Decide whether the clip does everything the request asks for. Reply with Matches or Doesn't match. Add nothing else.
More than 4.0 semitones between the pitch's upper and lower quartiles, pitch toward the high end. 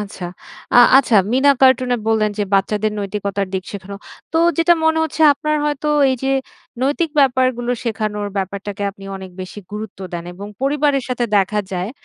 Matches